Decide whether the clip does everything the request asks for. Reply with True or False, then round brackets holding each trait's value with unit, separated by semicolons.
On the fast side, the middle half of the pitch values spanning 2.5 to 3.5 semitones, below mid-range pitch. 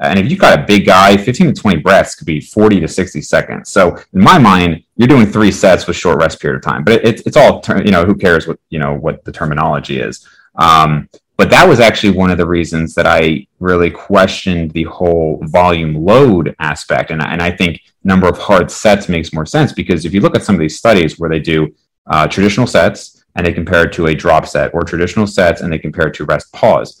True (245 wpm; 2.8 semitones; 85 Hz)